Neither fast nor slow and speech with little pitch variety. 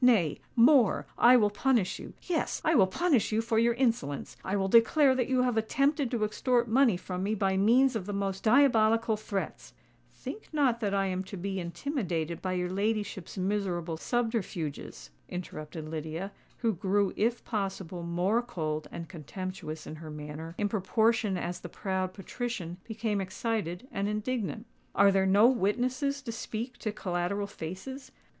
No: average, 160 wpm; average, 4.4 semitones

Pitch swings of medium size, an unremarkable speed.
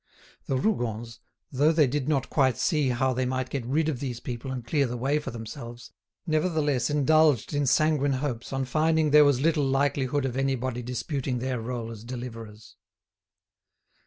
Yes: average, 3.2 semitones; average, 170 wpm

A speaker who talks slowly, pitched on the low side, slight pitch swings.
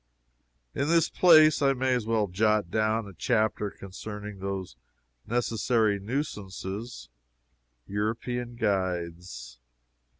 No: slow, 100 wpm; low, 110 Hz; average, 3.9 semitones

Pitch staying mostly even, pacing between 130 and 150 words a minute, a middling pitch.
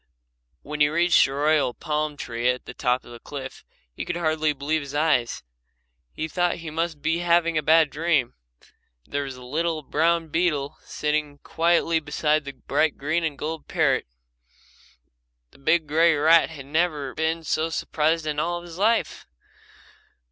No: narrow, 2.3 semitones; average, 165 wpm; medium, 155 Hz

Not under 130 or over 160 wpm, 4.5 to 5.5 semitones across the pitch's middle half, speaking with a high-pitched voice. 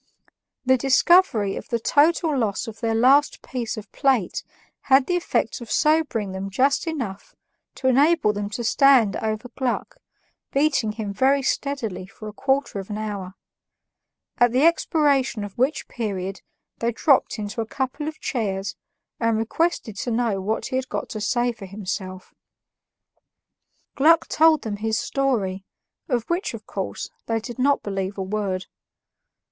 Yes: average, 155 wpm; average, 4.9 semitones; high, 235 Hz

